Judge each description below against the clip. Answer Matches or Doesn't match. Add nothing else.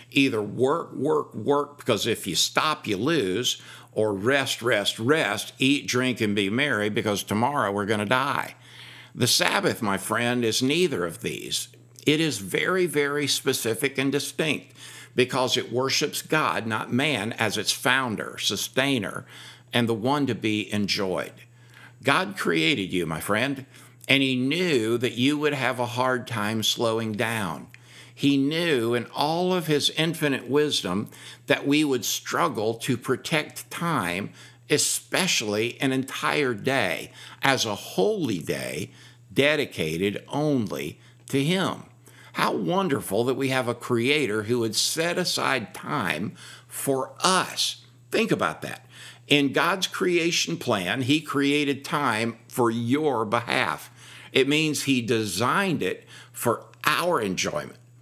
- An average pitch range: Matches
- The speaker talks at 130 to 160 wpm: Matches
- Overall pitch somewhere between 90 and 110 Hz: Doesn't match